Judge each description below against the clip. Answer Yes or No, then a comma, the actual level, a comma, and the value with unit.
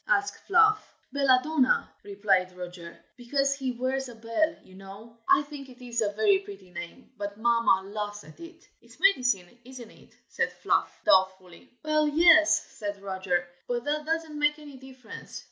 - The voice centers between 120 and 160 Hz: No, very high, 250 Hz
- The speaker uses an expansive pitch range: Yes, wide, 6.7 semitones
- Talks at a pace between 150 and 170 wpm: Yes, average, 160 wpm